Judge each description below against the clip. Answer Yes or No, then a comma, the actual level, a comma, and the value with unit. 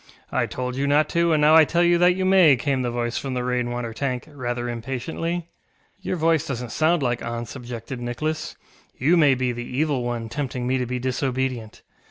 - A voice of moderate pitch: No, low, 130 Hz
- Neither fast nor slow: No, fast, 210 wpm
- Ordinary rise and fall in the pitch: Yes, average, 4.2 semitones